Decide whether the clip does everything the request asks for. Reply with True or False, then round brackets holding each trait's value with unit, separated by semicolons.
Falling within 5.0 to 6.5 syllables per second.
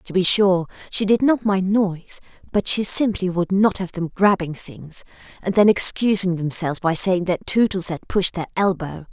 False (4.8 syllables/s)